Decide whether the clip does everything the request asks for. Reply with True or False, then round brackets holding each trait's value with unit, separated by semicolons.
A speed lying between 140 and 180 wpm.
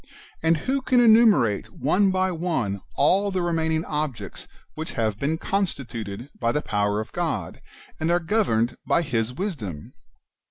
True (155 wpm)